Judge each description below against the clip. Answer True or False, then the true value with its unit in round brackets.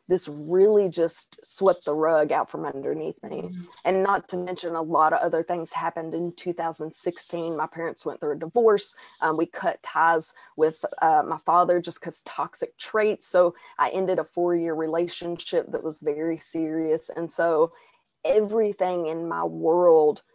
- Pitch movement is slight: True (2.3 semitones)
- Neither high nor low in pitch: True (170 Hz)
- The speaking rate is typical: True (165 wpm)